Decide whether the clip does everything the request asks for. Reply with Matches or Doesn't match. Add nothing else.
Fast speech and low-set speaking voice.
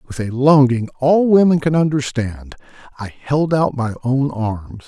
Doesn't match